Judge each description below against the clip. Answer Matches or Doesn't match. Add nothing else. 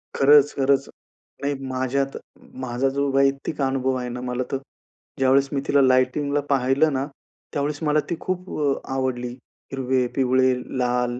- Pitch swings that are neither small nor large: Doesn't match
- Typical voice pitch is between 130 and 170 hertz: Matches